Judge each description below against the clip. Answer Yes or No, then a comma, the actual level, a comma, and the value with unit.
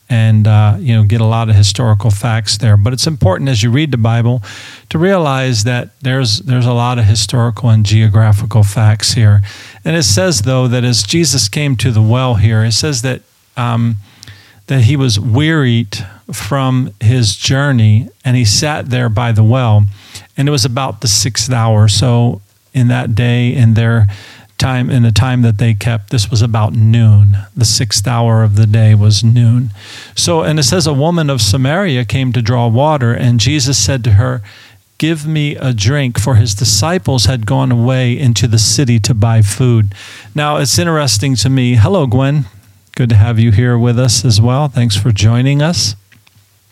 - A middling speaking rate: Yes, average, 190 wpm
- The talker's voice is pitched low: Yes, low, 120 Hz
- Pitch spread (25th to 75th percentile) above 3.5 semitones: No, average, 3.2 semitones